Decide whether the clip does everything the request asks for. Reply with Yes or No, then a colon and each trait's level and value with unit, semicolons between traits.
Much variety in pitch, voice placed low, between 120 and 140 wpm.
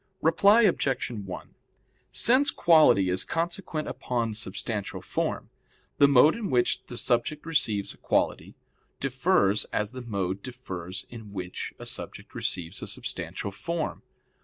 Yes: wide, 7.9 semitones; low, 120 Hz; slow, 135 wpm